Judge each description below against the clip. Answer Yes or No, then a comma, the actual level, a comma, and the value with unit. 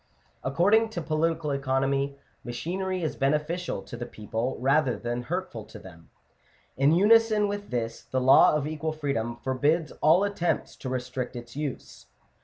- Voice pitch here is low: No, medium, 145 Hz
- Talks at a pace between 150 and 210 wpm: Yes, average, 155 wpm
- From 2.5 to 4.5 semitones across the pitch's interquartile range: No, average, 5.2 semitones